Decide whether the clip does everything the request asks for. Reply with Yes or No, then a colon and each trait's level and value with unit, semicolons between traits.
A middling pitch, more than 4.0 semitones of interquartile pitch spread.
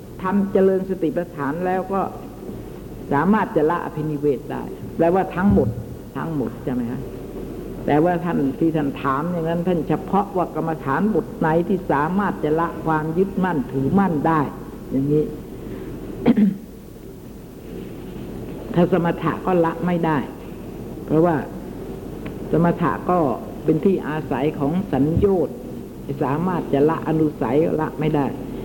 No: medium, 165 Hz; average, 3.5 semitones